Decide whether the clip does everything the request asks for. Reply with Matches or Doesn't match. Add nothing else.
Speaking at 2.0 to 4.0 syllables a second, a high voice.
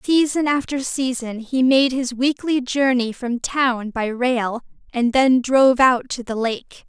Matches